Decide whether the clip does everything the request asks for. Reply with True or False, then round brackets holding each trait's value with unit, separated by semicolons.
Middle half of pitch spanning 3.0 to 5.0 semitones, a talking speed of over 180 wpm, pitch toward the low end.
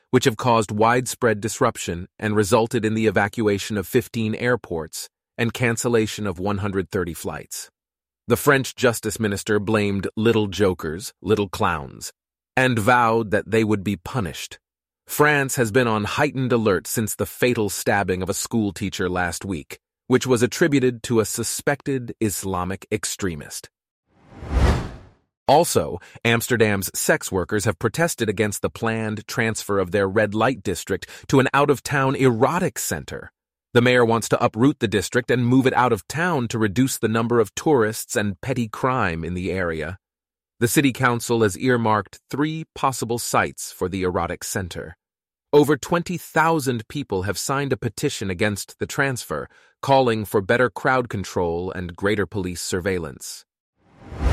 False (4.0 semitones; 150 wpm; 115 Hz)